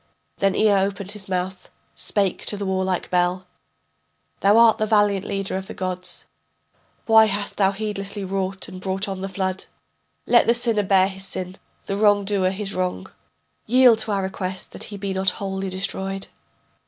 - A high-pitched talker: Yes, high, 195 Hz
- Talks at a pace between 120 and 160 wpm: No, average, 170 wpm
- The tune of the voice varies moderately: No, narrow, 1.5 semitones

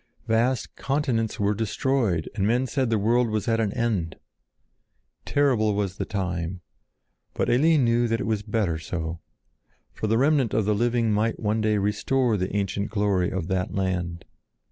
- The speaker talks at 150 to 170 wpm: Yes, average, 165 wpm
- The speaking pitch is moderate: No, low, 110 Hz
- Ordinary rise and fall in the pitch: Yes, average, 3.3 semitones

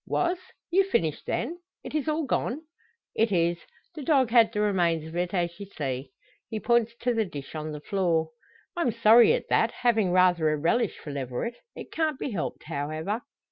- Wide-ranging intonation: Yes, wide, 6.9 semitones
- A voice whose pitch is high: Yes, high, 200 Hz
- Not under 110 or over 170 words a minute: No, average, 190 wpm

